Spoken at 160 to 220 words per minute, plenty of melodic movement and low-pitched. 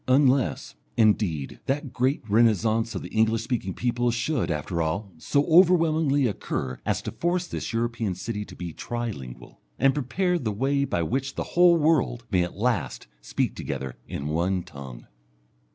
Yes: average, 165 wpm; wide, 7.0 semitones; low, 115 Hz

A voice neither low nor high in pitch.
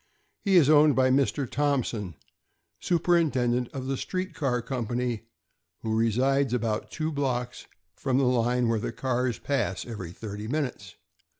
No: low, 125 Hz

